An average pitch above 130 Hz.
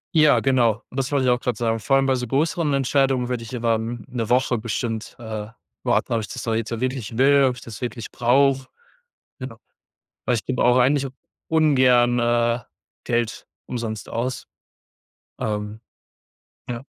No: low, 125 Hz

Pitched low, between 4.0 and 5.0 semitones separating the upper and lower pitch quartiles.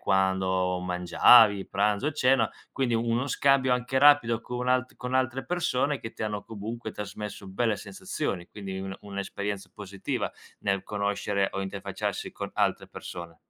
Yes: low, 105 Hz; average, 4.5 semitones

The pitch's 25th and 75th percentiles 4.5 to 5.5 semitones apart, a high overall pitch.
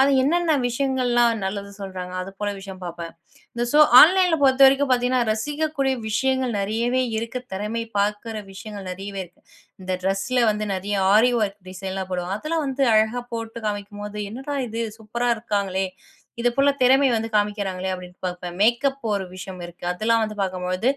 Yes: average, 4.8 semitones; high, 215 Hz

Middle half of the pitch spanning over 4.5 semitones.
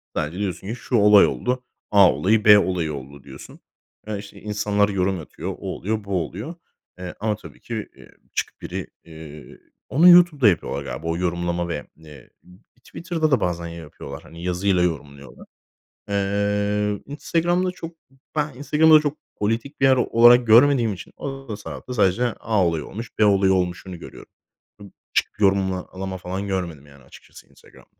Yes: wide, 5.4 semitones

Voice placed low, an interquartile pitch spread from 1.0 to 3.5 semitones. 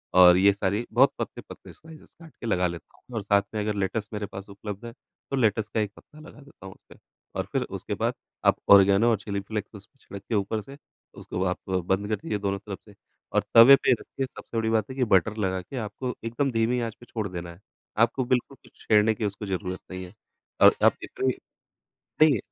Yes: low, 105 Hz; average, 3.2 semitones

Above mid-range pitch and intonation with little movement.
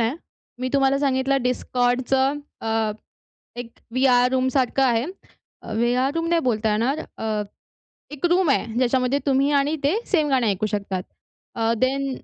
Yes: very high, 260 Hz; narrow, 2.3 semitones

